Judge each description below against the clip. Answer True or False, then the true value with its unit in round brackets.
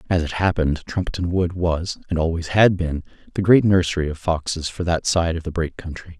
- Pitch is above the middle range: False (85 Hz)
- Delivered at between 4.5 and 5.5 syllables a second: False (5.8 syllables/s)